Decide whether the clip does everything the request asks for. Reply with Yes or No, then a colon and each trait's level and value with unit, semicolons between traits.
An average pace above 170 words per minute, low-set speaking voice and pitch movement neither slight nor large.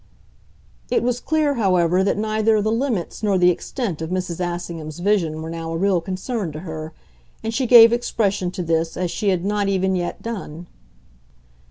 No: average, 180 wpm; high, 190 Hz; average, 4.3 semitones